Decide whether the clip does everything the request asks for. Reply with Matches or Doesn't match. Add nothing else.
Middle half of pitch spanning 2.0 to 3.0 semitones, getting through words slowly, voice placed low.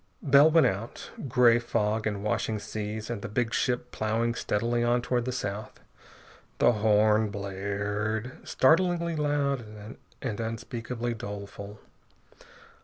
Matches